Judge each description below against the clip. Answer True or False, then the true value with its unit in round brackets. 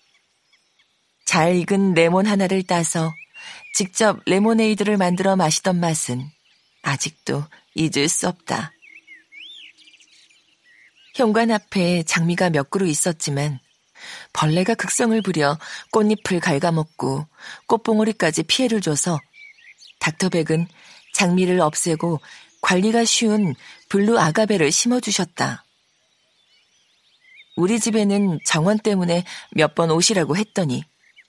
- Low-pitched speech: False (180 Hz)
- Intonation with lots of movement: False (4.6 semitones)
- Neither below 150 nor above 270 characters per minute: True (230 characters per minute)